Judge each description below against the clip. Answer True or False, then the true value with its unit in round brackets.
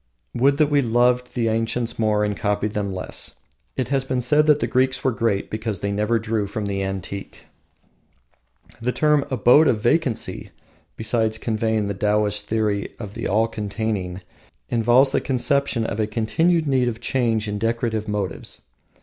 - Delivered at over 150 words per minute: True (165 wpm)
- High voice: False (115 Hz)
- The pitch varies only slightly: False (3.1 semitones)